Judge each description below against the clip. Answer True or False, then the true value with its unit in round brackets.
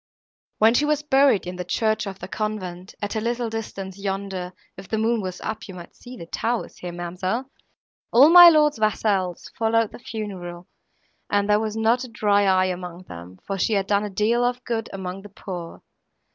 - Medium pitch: False (205 Hz)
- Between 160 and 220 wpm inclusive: True (200 wpm)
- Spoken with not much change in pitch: False (3.6 semitones)